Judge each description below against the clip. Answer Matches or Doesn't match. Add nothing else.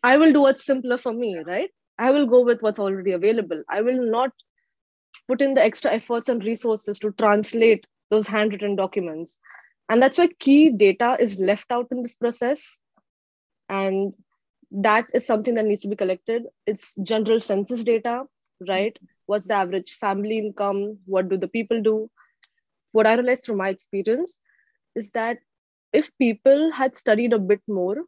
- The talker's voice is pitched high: Matches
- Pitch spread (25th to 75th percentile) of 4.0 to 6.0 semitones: Doesn't match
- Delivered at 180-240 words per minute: Doesn't match